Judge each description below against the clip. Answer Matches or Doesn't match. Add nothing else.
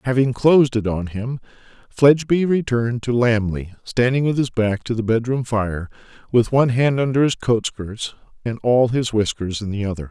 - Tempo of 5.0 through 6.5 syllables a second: Matches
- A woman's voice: Doesn't match